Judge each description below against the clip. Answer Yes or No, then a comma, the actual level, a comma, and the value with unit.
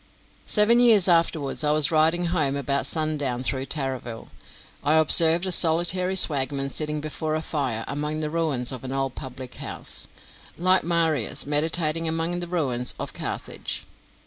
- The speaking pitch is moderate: Yes, medium, 155 Hz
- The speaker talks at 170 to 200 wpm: No, average, 155 wpm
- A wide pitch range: No, average, 3.5 semitones